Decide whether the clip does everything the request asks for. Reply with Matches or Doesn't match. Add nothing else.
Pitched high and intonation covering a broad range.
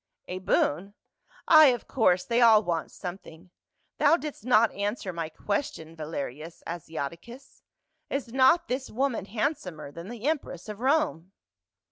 Matches